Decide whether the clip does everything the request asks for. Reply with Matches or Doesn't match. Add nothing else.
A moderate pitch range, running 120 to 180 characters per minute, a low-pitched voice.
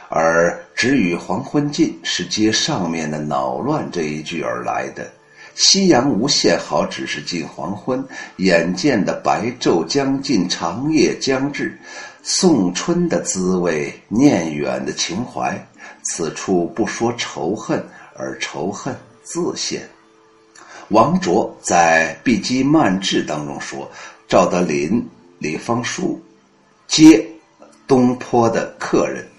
Doesn't match